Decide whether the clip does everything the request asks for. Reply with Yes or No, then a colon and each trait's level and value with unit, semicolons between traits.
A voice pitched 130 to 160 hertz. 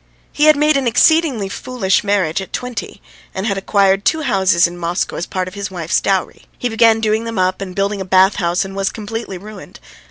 No: high, 200 Hz